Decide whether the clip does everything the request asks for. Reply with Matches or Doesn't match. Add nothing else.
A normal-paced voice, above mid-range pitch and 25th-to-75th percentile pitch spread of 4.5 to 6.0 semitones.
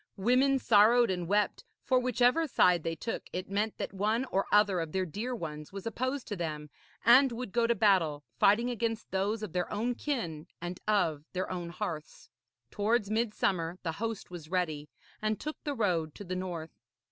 Matches